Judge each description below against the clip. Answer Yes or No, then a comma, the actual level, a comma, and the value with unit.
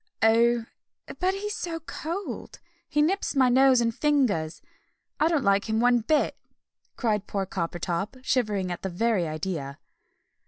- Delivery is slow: No, average, 145 wpm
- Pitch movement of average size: No, wide, 7.5 semitones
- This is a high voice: Yes, high, 230 Hz